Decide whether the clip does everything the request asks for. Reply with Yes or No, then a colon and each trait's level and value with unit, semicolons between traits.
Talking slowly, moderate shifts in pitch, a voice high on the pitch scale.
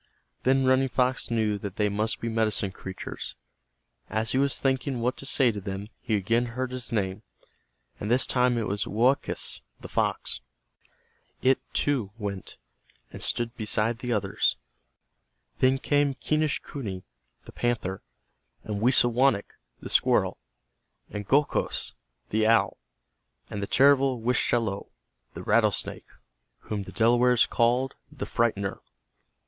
No: slow, 130 wpm; average, 3.8 semitones; low, 115 Hz